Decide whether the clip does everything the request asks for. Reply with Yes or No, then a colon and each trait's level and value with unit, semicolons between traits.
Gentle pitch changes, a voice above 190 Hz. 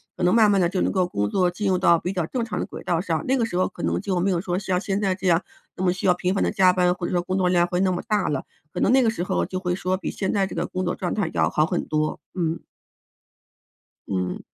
No: narrow, 1.6 semitones; medium, 185 Hz